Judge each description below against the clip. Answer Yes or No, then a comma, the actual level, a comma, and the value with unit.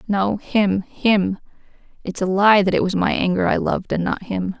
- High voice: Yes, high, 195 Hz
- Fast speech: Yes, fast, 210 wpm